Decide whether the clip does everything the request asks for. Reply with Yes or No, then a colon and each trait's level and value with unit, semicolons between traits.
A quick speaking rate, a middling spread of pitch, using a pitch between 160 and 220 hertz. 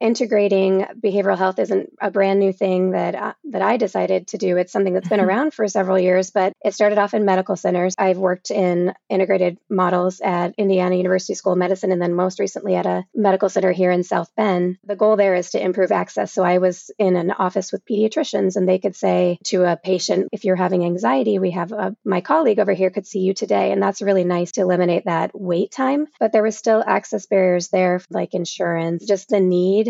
No: fast, 225 wpm; narrow, 1.9 semitones; high, 190 Hz